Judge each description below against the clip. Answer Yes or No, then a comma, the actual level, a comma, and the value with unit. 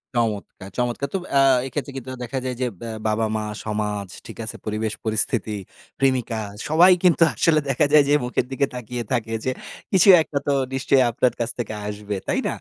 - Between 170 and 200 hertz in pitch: No, low, 120 Hz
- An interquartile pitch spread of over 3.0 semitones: Yes, average, 4.1 semitones